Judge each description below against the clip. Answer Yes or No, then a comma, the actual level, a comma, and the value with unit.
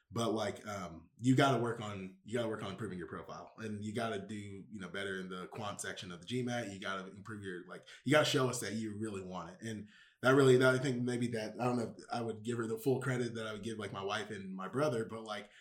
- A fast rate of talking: Yes, fast, 300 wpm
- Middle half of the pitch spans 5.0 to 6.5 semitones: No, average, 3.8 semitones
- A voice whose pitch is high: No, low, 110 Hz